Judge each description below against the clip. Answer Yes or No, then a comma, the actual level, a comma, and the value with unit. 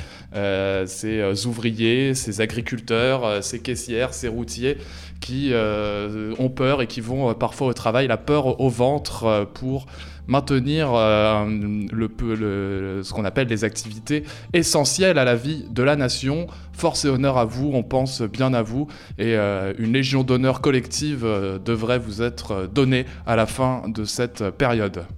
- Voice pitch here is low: Yes, low, 115 Hz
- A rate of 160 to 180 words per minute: Yes, average, 170 wpm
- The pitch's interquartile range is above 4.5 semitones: No, average, 3.7 semitones